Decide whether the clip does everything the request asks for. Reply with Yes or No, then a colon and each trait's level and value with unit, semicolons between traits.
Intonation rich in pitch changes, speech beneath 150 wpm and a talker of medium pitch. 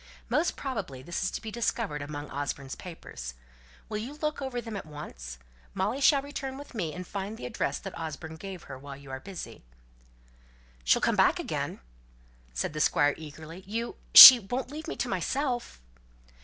No: wide, 9.0 semitones; average, 185 wpm; medium, 180 Hz